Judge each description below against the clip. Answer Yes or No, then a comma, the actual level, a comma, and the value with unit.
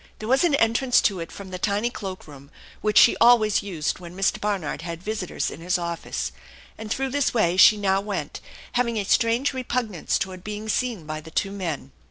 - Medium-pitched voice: No, high, 205 Hz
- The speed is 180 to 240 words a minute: Yes, fast, 205 wpm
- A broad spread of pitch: No, average, 4.4 semitones